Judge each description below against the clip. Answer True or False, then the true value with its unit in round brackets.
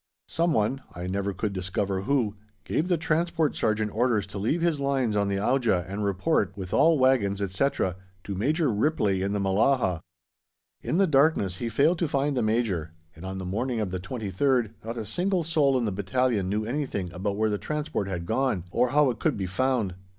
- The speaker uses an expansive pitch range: True (5.9 semitones)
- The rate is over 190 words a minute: True (200 wpm)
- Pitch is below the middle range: True (110 Hz)